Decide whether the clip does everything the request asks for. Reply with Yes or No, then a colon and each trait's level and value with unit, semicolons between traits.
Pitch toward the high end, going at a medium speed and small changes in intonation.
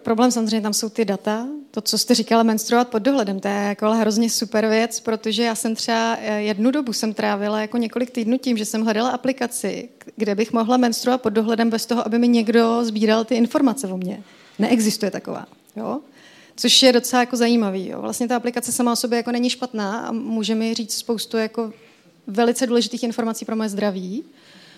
No: high, 230 Hz; fast, 195 wpm; narrow, 1.8 semitones